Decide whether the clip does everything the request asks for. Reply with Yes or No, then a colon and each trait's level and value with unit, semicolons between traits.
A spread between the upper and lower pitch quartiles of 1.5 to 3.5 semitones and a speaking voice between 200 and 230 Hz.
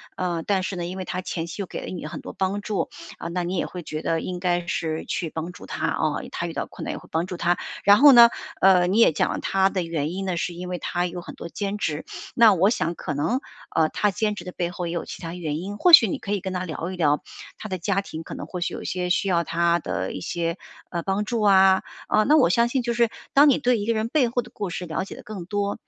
No: average, 3.1 semitones; medium, 185 Hz